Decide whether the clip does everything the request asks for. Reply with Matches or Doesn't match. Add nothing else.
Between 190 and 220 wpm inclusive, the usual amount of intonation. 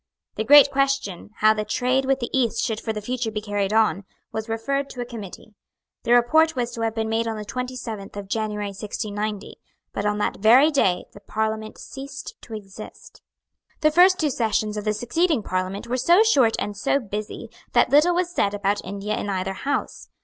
Matches